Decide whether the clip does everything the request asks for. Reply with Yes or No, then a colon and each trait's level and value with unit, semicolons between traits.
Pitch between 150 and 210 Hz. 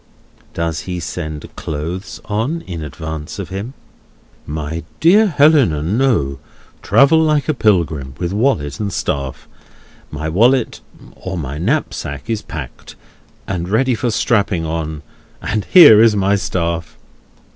No: very low, 90 Hz